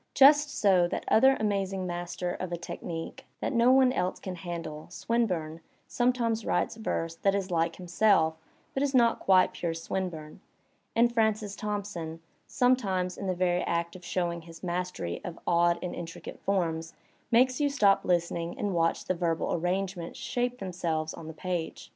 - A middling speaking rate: Yes, average, 165 wpm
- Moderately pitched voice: Yes, medium, 180 Hz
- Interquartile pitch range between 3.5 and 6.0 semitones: Yes, average, 4.3 semitones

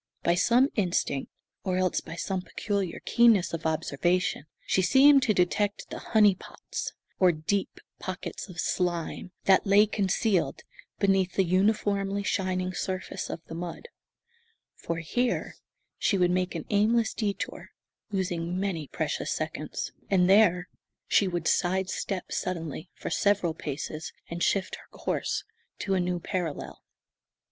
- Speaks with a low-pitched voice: No, medium, 185 Hz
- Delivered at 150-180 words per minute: No, average, 140 wpm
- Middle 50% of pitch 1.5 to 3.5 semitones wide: Yes, narrow, 2.5 semitones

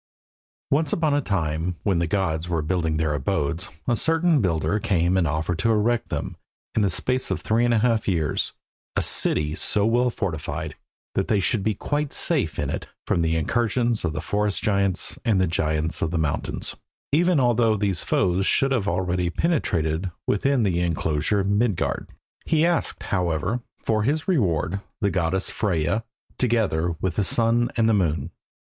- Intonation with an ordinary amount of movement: No, wide, 6.0 semitones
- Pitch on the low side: Yes, low, 100 Hz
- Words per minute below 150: No, average, 165 wpm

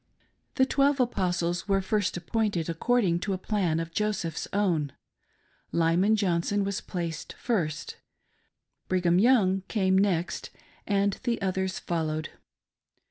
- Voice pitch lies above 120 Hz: Yes, high, 190 Hz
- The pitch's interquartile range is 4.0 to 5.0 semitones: No, average, 3.5 semitones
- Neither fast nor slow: No, slow, 130 wpm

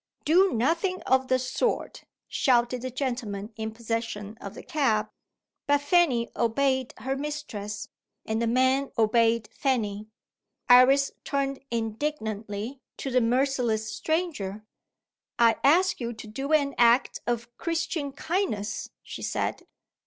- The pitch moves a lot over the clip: No, average, 3.9 semitones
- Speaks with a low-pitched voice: No, very high, 250 Hz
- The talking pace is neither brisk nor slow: No, slow, 125 wpm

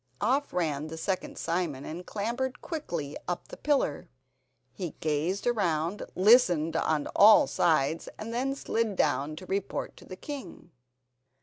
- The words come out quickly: No, average, 140 wpm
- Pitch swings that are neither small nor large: No, wide, 6.6 semitones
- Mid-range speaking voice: Yes, medium, 180 Hz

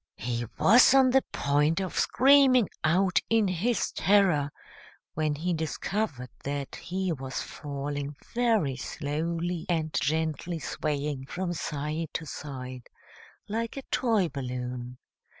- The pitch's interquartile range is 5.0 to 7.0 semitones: Yes, average, 5.3 semitones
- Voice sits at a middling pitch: Yes, medium, 160 Hz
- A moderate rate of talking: No, slow, 120 wpm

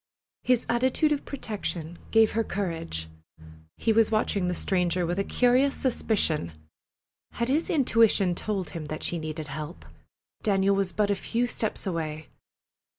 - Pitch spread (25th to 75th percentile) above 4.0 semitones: Yes, average, 5.3 semitones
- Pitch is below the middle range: No, high, 200 Hz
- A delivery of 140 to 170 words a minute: Yes, average, 150 wpm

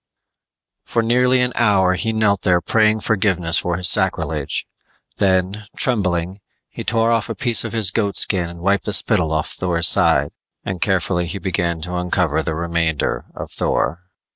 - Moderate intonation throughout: Yes, average, 4.1 semitones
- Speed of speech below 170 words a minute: Yes, average, 160 wpm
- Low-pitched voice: Yes, very low, 95 Hz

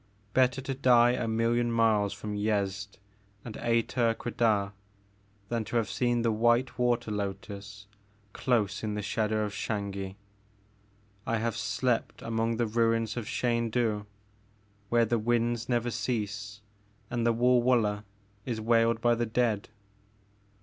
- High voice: No, low, 115 Hz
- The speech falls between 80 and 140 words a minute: Yes, slow, 135 wpm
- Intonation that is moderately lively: No, narrow, 2.2 semitones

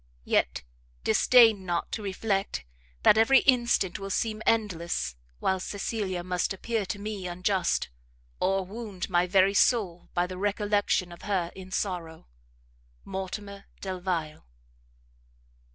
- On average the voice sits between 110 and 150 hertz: No, high, 195 Hz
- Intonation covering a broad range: No, narrow, 2.6 semitones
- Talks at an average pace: No, slow, 120 wpm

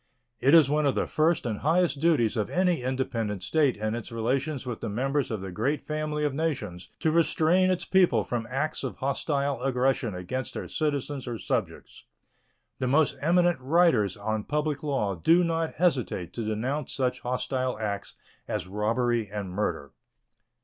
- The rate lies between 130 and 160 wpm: No, average, 170 wpm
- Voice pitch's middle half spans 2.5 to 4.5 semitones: No, wide, 5.6 semitones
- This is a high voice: No, low, 130 Hz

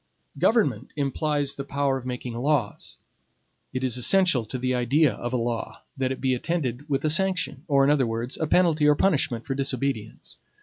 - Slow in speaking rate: No, average, 185 wpm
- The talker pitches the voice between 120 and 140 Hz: Yes, low, 135 Hz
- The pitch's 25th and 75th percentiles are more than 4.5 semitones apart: No, average, 3.1 semitones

